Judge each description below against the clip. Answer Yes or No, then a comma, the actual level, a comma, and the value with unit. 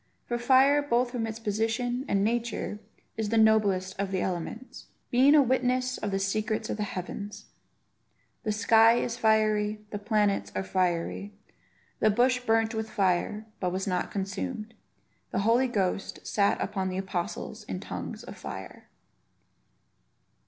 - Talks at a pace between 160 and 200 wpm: No, average, 150 wpm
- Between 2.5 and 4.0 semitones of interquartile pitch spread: Yes, average, 3.3 semitones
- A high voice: Yes, high, 215 Hz